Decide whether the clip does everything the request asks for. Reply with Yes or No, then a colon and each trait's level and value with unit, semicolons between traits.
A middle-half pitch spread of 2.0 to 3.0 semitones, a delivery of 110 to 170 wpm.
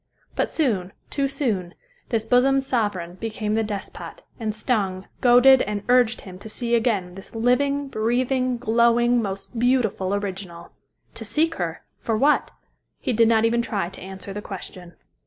No: average, 4.1 semitones; average, 155 wpm